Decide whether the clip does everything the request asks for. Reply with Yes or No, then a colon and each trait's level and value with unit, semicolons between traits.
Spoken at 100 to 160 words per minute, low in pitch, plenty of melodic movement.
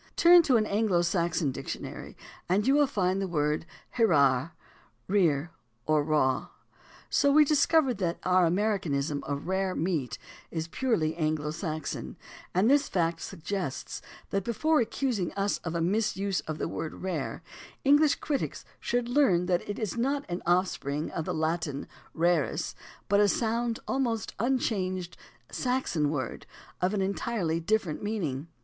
No: average, 150 wpm; medium, 185 Hz; wide, 5.9 semitones